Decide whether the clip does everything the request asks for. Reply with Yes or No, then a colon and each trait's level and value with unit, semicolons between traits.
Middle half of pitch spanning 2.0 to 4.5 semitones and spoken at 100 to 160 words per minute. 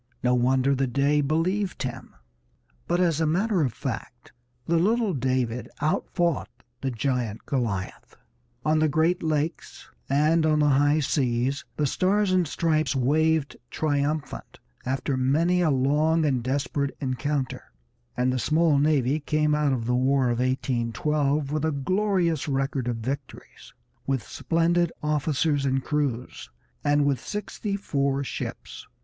Yes: average, 3.2 semitones; average, 140 wpm